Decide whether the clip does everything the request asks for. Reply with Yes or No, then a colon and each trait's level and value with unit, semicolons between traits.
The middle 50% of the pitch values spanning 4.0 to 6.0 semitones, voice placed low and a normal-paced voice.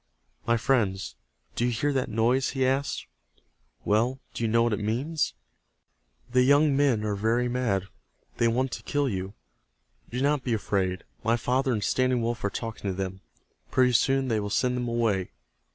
No: average, 3.4 semitones; low, 120 Hz; average, 180 wpm